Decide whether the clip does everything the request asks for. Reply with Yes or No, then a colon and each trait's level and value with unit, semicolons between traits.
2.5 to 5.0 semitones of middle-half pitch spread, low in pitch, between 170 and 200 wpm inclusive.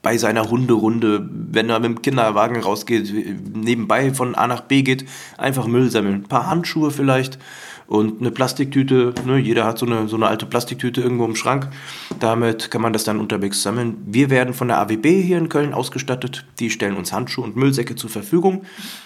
Yes: average, 2.9 semitones; low, 120 Hz; fast, 190 wpm